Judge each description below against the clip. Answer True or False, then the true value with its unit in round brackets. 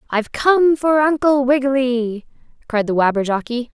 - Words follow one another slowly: True (125 wpm)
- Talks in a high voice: True (260 Hz)